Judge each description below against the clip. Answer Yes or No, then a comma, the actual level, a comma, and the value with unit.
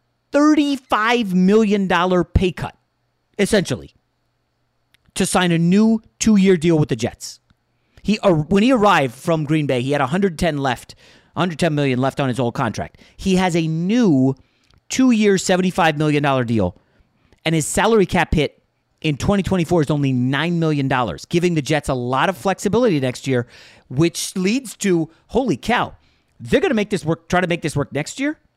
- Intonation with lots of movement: Yes, wide, 6.3 semitones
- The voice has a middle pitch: Yes, medium, 165 Hz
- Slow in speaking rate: No, average, 170 wpm